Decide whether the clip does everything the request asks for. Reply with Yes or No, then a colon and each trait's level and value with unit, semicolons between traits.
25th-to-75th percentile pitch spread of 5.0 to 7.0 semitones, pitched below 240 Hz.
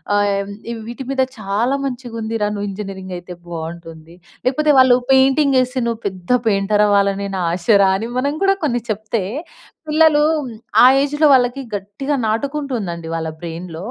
Yes: average, 5.3 semitones; high, 215 Hz